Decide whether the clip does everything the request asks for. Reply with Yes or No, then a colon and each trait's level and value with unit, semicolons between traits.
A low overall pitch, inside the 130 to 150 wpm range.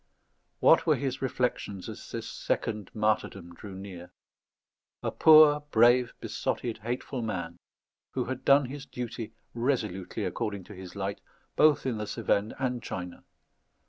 Yes: low, 115 Hz; average, 140 wpm